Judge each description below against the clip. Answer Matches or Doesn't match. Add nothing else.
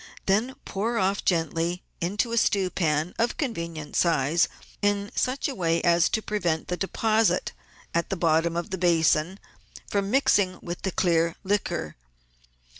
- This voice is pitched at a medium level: Matches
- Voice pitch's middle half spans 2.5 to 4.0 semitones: Matches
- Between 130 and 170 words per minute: Matches